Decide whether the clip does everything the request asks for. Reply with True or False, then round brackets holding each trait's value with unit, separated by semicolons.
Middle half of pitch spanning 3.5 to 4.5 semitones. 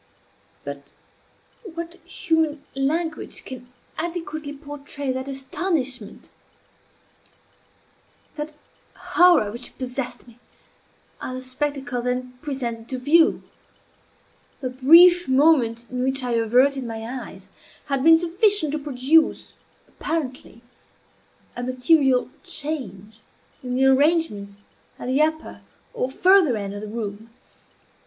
True (4.1 semitones)